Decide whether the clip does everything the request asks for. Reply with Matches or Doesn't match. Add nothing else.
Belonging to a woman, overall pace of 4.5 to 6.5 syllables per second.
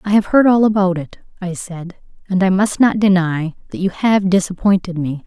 Matches